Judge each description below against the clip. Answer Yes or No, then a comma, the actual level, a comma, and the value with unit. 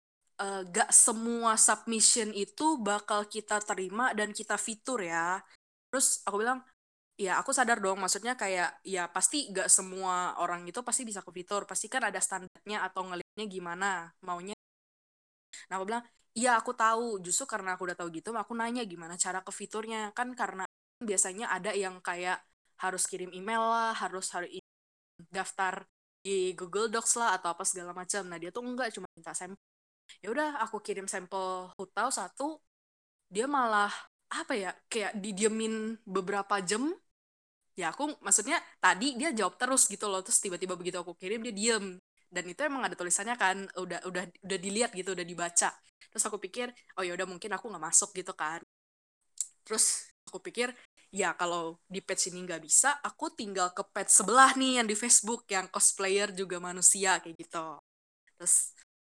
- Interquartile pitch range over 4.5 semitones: No, average, 3.6 semitones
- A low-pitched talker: No, high, 200 Hz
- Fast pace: Yes, fast, 170 wpm